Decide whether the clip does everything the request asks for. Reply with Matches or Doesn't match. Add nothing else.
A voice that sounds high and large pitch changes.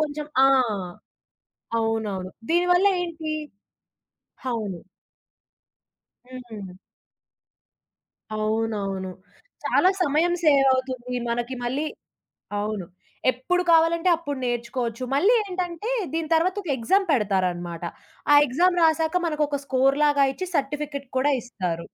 Matches